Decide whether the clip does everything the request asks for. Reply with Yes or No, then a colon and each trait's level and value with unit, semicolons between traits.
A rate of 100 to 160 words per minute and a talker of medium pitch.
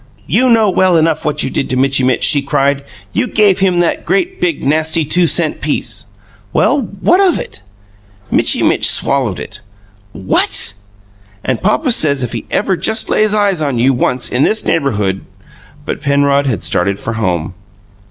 No: average, 175 wpm; medium, 145 Hz